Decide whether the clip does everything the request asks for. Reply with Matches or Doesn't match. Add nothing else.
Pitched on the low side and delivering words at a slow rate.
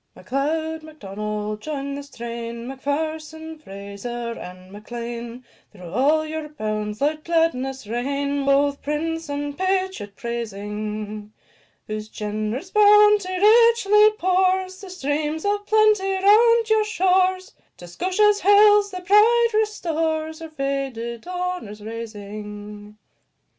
Doesn't match